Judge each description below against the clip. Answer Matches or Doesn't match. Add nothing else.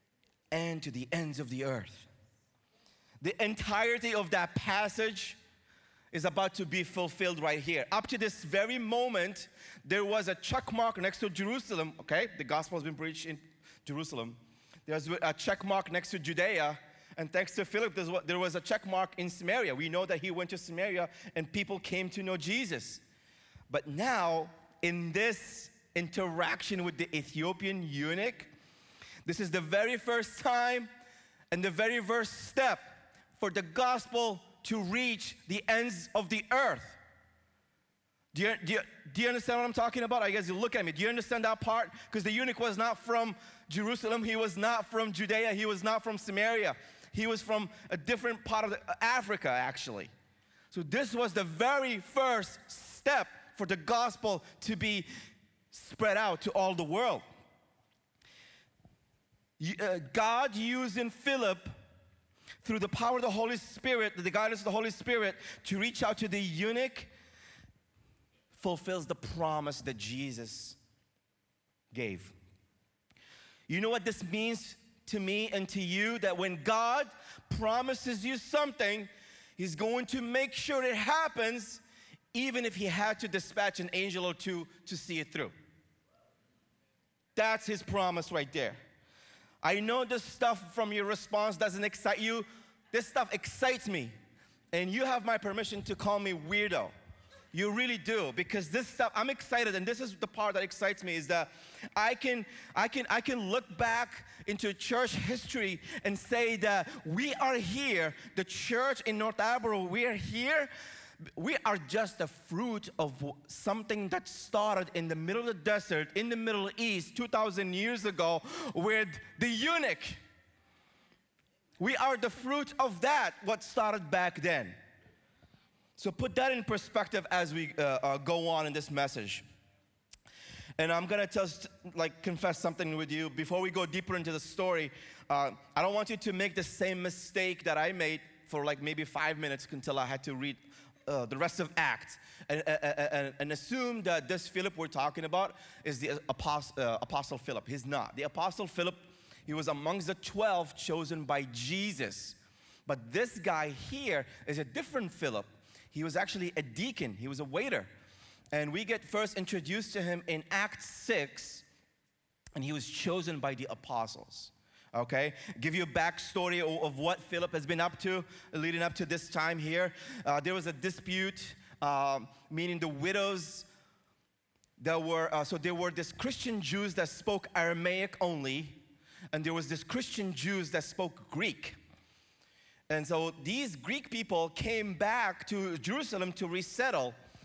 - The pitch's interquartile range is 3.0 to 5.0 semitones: Doesn't match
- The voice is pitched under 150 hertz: Doesn't match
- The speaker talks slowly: Doesn't match